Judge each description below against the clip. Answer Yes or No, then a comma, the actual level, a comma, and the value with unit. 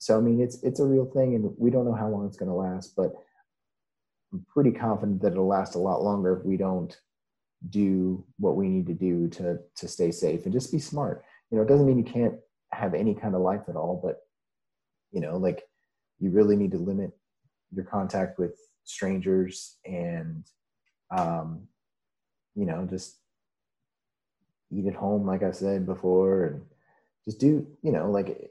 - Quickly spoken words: No, average, 190 wpm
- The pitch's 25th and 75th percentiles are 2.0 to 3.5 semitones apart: No, wide, 5.5 semitones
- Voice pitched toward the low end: Yes, low, 100 Hz